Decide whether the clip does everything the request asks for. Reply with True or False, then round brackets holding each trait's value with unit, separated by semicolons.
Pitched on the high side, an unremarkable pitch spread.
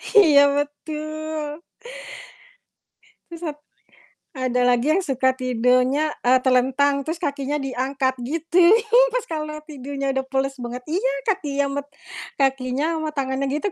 True (280 Hz; 3.0 semitones)